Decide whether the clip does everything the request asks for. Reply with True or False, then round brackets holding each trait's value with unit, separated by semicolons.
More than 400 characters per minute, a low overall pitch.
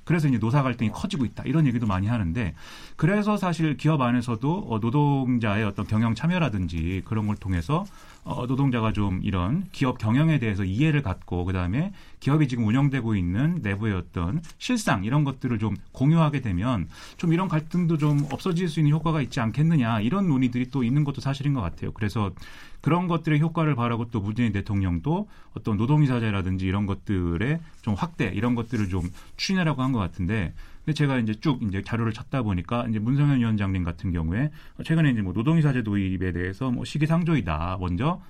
True (410 characters per minute; 120 Hz)